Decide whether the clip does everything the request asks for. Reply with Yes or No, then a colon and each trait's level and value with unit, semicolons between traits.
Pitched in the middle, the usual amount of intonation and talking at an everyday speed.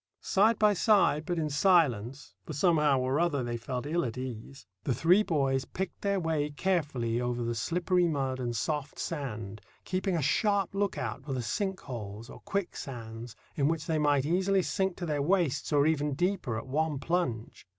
No: medium, 145 Hz; wide, 5.8 semitones; average, 180 wpm